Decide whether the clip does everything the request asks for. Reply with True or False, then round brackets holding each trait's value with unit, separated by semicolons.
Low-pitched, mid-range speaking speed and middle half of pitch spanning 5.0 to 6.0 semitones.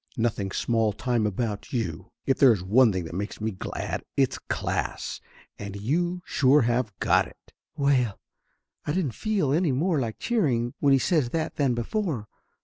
True (125 Hz; 165 wpm; 5.5 semitones)